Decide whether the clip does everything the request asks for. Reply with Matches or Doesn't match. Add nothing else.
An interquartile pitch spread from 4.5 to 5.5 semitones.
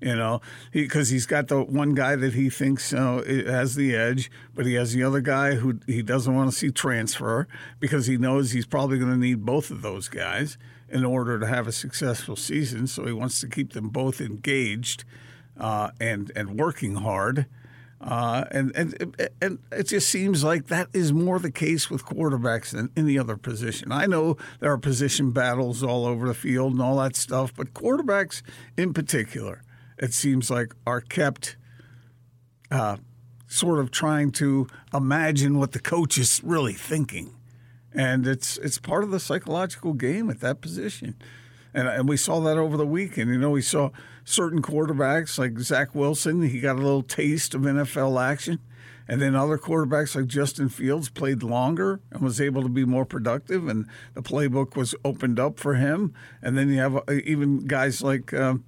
Doesn't match